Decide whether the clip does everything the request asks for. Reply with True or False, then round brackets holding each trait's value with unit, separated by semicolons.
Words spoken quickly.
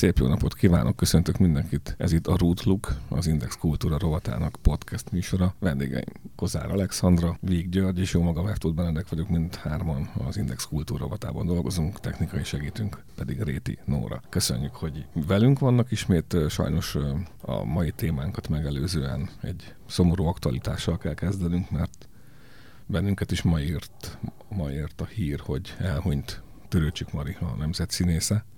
False (145 wpm)